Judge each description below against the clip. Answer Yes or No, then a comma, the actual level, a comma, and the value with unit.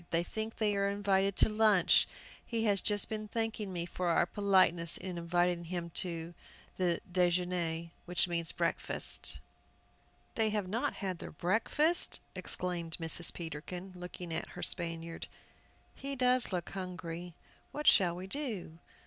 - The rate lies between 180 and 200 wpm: No, average, 140 wpm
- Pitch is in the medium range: Yes, medium, 180 Hz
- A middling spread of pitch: Yes, average, 3.3 semitones